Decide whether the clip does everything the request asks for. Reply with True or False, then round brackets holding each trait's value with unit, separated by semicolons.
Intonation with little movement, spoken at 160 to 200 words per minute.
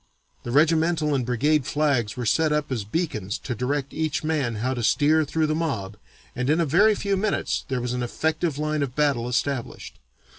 False (4.2 semitones; 195 wpm)